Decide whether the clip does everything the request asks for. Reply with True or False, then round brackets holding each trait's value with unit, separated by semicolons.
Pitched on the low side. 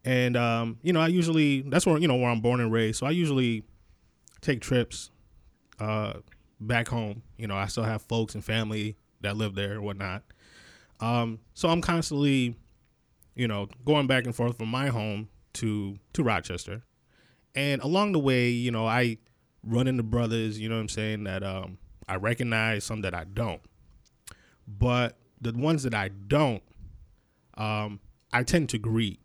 True (115 Hz)